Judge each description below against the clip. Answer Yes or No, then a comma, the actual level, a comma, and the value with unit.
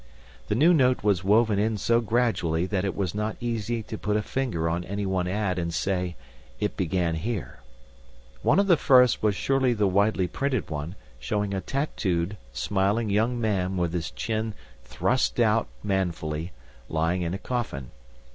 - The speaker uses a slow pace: No, average, 170 wpm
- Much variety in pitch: No, average, 4.3 semitones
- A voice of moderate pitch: No, low, 100 Hz